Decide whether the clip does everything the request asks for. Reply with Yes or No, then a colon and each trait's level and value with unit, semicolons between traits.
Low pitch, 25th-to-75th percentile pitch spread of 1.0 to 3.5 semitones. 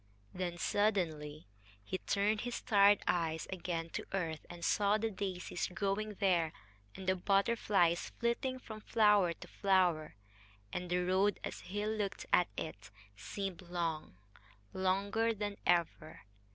No: high, 190 Hz; average, 3.1 semitones